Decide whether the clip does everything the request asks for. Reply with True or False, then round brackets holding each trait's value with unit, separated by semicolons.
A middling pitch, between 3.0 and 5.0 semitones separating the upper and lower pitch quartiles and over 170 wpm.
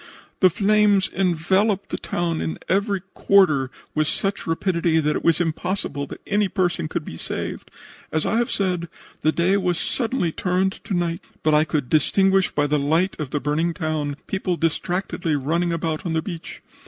True (170 Hz; 3.5 semitones; 180 wpm)